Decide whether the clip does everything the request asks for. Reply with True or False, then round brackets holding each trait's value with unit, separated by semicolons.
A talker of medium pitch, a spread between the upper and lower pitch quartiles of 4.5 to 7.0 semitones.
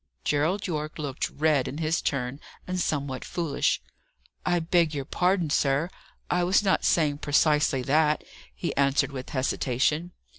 False (150 Hz; 3.5 semitones)